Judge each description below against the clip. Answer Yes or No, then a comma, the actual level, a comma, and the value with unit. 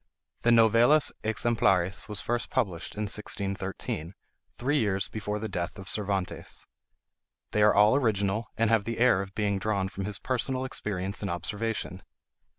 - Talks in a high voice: No, low, 105 Hz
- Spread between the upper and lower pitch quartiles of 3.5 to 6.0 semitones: No, average, 2.8 semitones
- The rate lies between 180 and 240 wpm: No, average, 155 wpm